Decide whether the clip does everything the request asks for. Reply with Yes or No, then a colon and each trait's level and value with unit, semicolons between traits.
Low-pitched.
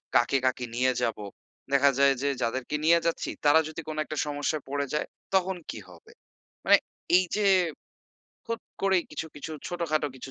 No: medium, 150 Hz